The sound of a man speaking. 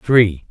Yes: male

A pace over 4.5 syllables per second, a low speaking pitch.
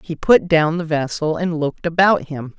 No: 4.8 syllables/s; medium, 160 Hz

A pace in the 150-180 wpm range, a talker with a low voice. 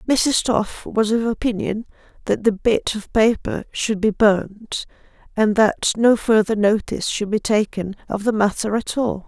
No: average, 170 wpm; high, 215 Hz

